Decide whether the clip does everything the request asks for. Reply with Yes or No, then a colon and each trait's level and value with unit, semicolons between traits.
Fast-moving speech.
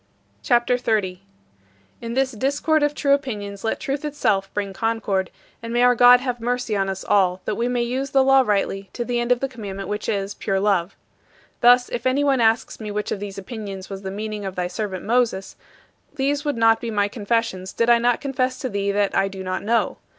Yes: fast, 215 wpm